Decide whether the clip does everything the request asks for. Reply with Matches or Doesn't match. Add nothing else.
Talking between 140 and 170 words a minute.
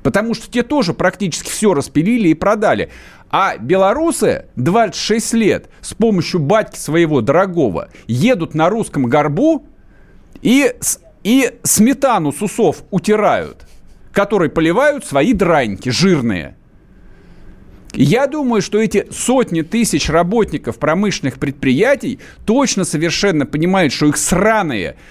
Doesn't match